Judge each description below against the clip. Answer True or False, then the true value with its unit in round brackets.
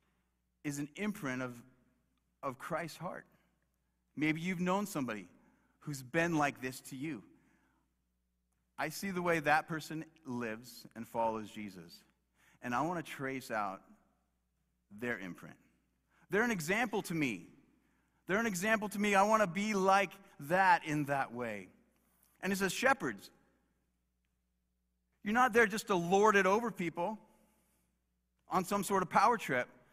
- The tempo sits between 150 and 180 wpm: False (140 wpm)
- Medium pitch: True (150 Hz)